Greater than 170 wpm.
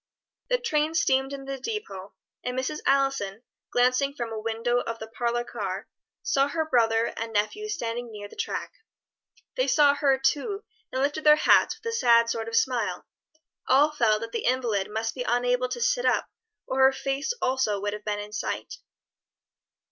Yes: average, 180 wpm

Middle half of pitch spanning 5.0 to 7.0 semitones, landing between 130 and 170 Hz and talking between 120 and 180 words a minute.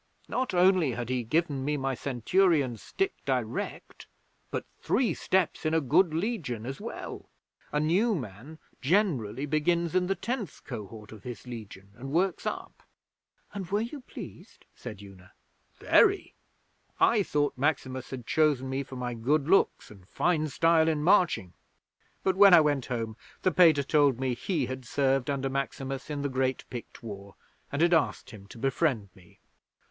Yes: wide, 5.6 semitones; medium, 140 Hz; average, 165 wpm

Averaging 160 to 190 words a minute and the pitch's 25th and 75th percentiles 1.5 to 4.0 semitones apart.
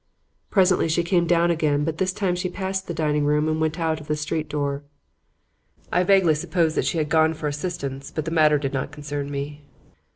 No: fast, 205 wpm; average, 2.7 semitones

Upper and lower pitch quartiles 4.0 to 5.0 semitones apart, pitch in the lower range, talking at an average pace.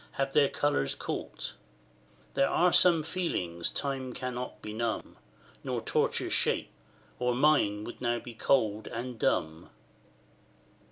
No: average, 4.3 semitones; low, 125 Hz; slow, 120 wpm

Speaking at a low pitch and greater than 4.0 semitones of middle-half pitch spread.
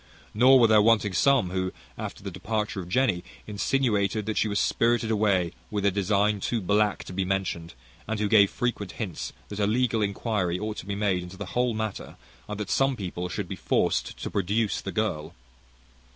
No: low, 105 Hz; narrow, 2.5 semitones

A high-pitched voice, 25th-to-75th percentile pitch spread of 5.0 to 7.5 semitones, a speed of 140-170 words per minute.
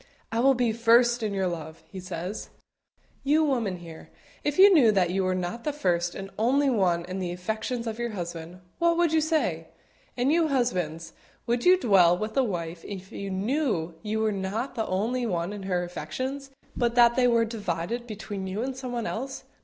No: high, 220 Hz; wide, 5.5 semitones; average, 200 wpm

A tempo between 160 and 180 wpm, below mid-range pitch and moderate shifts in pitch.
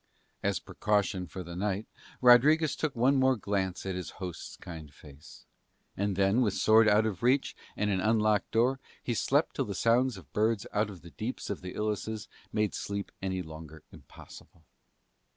Yes: average, 175 wpm; low, 105 Hz; average, 3.5 semitones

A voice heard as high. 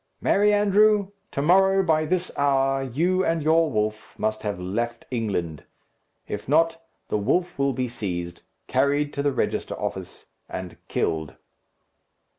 No: medium, 140 Hz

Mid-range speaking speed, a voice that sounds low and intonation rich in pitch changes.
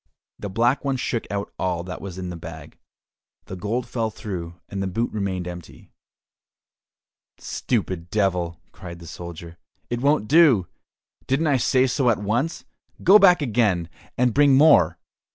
Yes: average, 155 wpm; low, 105 Hz; wide, 6.3 semitones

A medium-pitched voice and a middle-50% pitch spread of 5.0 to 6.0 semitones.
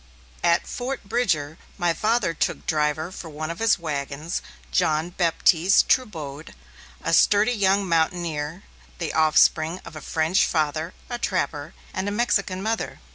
No: medium, 170 Hz; average, 4.2 semitones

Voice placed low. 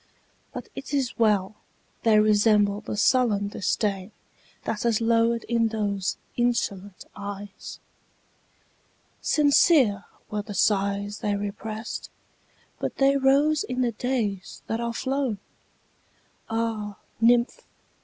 No: high, 220 Hz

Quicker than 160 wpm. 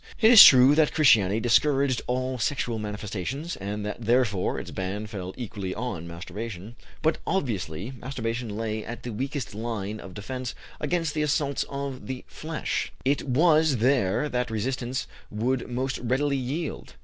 No: average, 150 wpm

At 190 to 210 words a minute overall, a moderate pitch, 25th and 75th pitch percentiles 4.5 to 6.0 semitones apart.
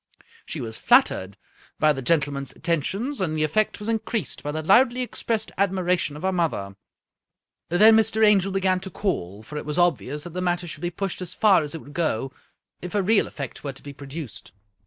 Yes: fast, 205 wpm; medium, 175 Hz; average, 5.2 semitones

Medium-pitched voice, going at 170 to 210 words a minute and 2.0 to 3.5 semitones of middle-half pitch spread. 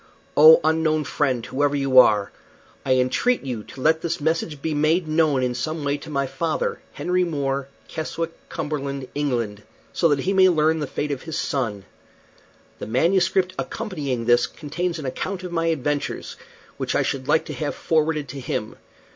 Yes: medium, 150 Hz; average, 175 wpm; average, 3.2 semitones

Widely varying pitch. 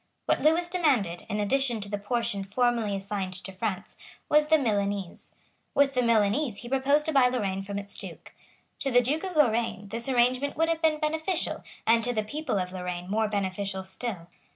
Yes: wide, 5.9 semitones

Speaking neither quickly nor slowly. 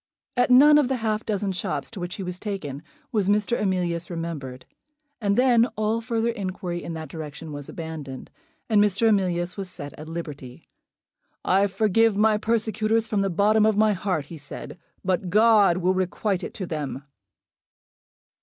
Yes: average, 170 wpm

